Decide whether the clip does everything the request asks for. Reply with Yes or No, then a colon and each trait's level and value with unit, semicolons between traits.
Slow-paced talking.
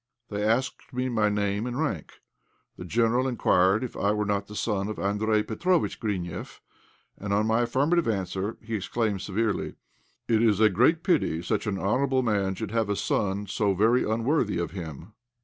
No: average, 180 wpm